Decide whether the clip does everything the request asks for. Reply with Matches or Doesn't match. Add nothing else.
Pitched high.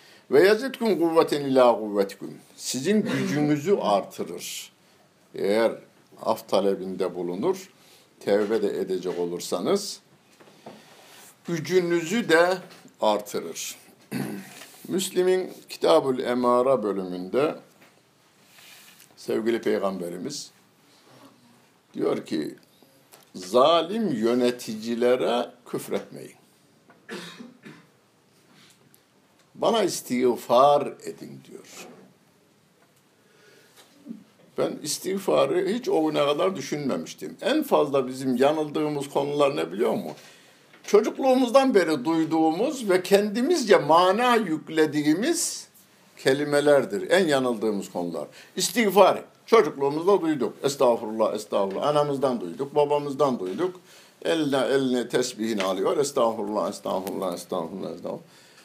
Doesn't match